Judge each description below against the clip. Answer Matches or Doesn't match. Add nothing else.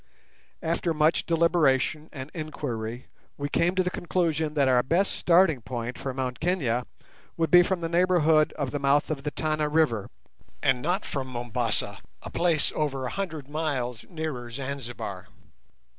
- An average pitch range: Matches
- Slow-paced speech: Doesn't match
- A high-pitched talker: Doesn't match